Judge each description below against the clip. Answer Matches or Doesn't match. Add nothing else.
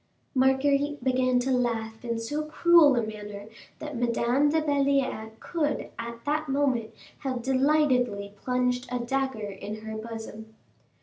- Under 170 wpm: Matches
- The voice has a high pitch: Matches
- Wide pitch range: Doesn't match